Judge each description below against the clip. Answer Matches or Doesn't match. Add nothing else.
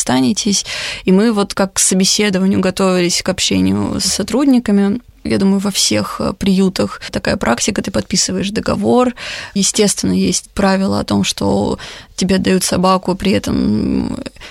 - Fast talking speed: Doesn't match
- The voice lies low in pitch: Doesn't match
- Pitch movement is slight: Matches